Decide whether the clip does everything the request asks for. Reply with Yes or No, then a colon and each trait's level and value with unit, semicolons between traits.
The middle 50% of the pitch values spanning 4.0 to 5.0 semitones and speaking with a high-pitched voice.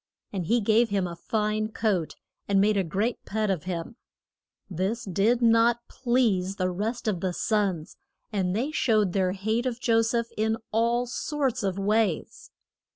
No: average, 3.5 semitones; high, 215 Hz